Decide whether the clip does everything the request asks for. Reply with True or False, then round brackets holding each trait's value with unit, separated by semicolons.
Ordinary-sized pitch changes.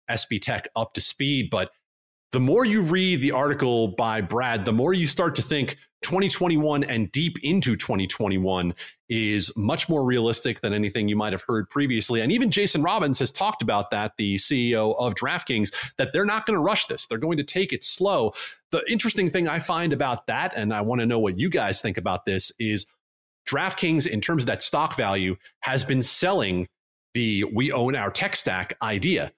False (6.4 semitones)